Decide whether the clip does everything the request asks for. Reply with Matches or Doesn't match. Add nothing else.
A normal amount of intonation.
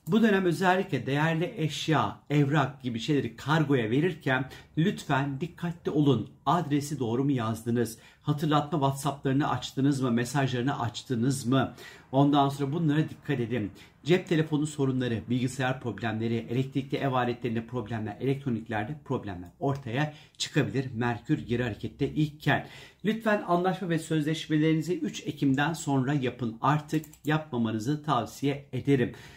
Matches